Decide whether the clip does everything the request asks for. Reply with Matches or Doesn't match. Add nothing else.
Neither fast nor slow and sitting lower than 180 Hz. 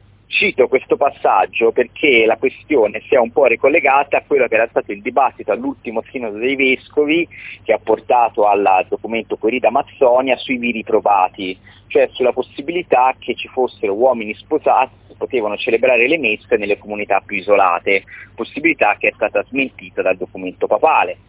Matches